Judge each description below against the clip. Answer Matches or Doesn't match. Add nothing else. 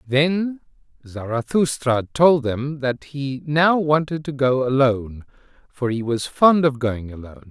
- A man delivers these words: Matches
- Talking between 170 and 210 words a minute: Doesn't match